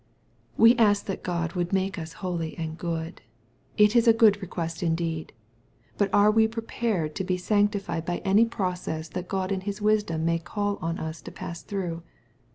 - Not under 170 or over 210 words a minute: Yes, average, 180 wpm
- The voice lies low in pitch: No, medium, 185 Hz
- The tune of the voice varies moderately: Yes, average, 3.7 semitones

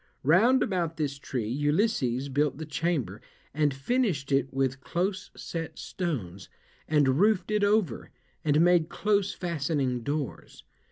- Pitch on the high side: No, medium, 150 Hz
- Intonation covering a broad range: No, average, 4.9 semitones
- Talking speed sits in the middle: No, slow, 130 wpm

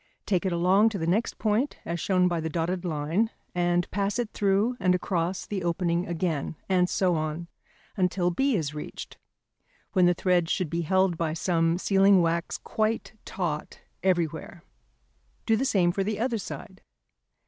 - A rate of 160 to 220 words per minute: Yes, average, 170 wpm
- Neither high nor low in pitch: Yes, medium, 180 Hz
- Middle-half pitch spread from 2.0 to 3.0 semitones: Yes, narrow, 2.6 semitones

